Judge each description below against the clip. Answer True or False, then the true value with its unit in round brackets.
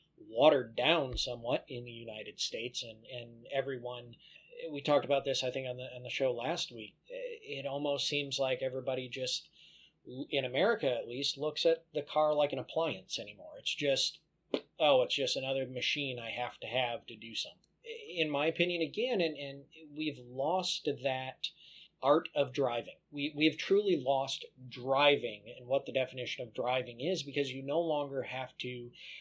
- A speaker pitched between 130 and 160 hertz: True (135 Hz)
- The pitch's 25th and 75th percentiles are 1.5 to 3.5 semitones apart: True (3.2 semitones)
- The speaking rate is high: False (175 wpm)